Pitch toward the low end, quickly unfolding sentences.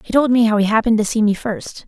No: high, 220 Hz; fast, 320 wpm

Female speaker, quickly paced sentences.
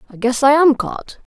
Yes: female; fast, 225 wpm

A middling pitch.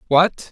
Yes: medium, 170 Hz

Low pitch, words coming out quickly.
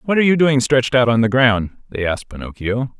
Yes: low, 125 Hz; fast, 240 wpm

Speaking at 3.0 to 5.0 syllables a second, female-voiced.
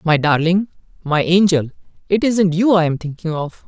No: 4.9 syllables/s; male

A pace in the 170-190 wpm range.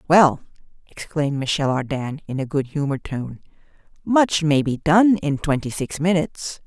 No: average, 155 wpm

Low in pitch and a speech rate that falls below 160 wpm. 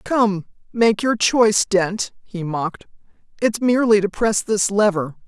No: high, 205 Hz; average, 150 wpm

